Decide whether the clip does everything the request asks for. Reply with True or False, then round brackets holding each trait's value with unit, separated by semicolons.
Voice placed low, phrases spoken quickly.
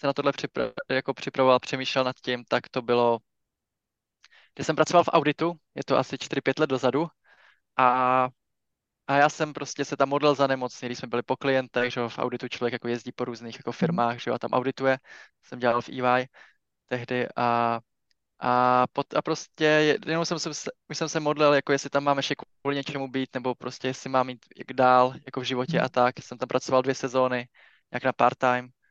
True (130 Hz; 200 wpm)